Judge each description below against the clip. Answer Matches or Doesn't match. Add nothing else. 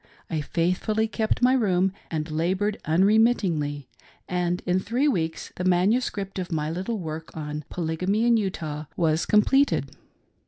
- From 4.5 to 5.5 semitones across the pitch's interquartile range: Matches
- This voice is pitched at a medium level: Matches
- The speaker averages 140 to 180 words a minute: Matches